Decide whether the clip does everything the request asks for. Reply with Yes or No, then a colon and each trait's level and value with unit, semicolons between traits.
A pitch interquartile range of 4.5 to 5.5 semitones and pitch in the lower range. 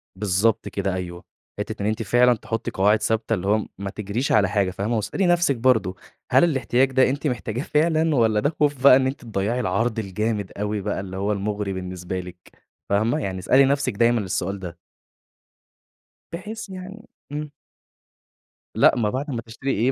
Yes: average, 5.0 semitones; low, 110 Hz